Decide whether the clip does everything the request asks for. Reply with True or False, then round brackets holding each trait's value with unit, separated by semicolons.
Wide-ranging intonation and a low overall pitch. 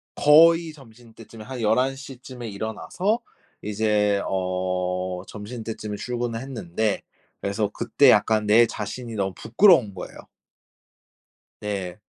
False (3.5 semitones; 110 Hz)